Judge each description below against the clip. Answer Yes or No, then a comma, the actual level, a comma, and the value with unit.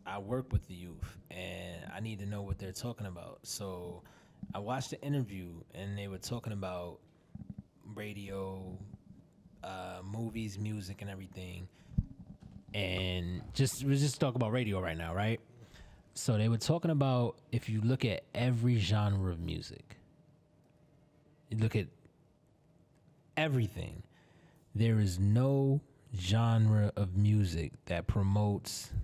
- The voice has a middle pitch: No, low, 105 Hz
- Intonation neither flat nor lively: Yes, average, 4.4 semitones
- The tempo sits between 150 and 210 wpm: No, slow, 135 wpm